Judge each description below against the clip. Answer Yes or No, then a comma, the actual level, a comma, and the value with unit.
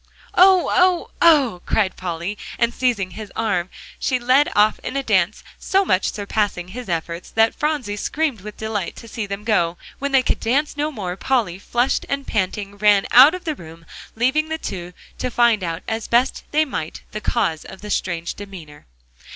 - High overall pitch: Yes, high, 215 Hz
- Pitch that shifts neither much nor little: No, wide, 6.0 semitones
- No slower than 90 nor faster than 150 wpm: No, average, 185 wpm